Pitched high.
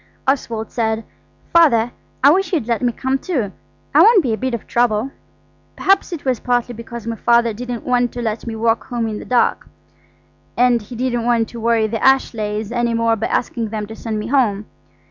Yes: high, 235 Hz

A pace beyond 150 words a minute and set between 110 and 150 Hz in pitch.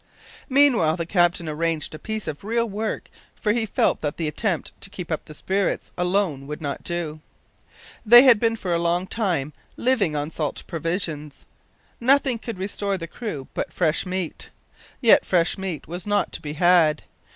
No: average, 175 wpm; medium, 180 Hz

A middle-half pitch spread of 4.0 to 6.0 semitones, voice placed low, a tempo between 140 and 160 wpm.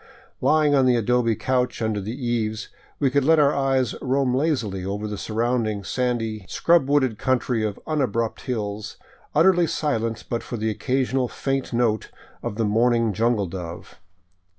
No: average, 3.5 semitones; low, 120 Hz; average, 155 wpm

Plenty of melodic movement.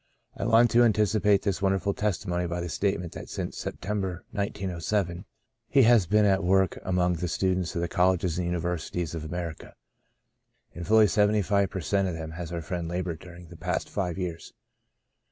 No: average, 2.7 semitones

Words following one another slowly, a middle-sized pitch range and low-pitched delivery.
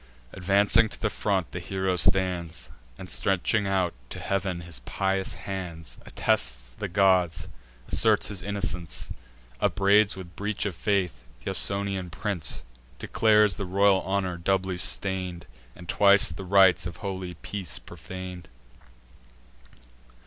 No: slow, 125 wpm; narrow, 2.1 semitones; very low, 95 Hz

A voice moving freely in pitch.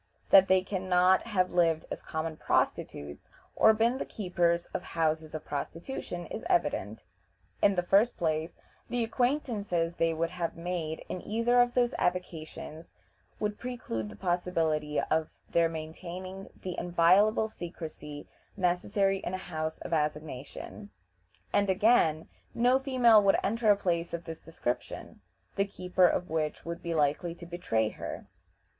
No: average, 3.8 semitones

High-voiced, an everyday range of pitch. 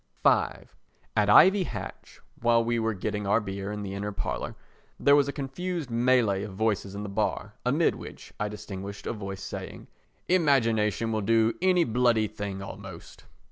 No: low, 110 Hz; average, 3.6 semitones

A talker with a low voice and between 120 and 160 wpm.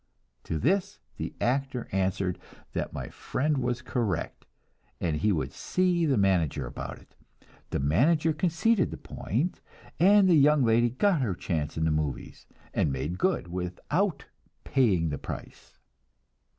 Yes: low, 120 Hz; average, 145 wpm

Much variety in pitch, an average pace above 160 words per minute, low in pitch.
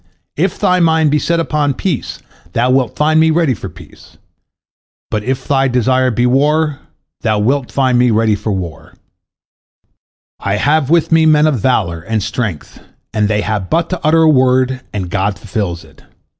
Yes: wide, 6.3 semitones; average, 170 wpm; low, 130 Hz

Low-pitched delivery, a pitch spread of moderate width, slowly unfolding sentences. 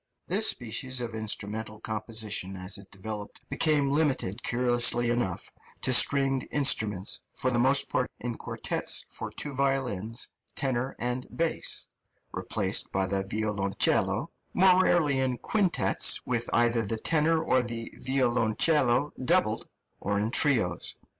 Yes: low, 120 Hz; average, 4.0 semitones; slow, 130 wpm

